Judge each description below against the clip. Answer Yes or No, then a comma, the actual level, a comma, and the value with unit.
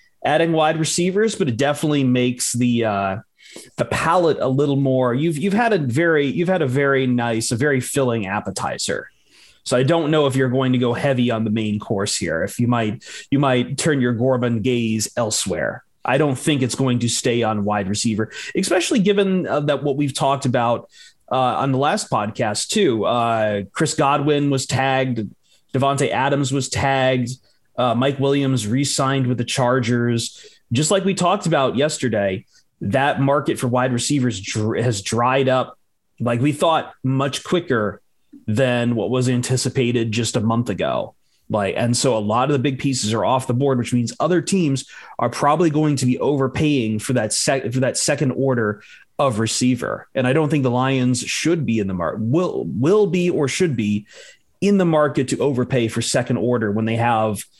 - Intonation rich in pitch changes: No, average, 3.3 semitones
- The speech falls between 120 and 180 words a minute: No, average, 190 wpm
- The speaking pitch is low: Yes, low, 130 Hz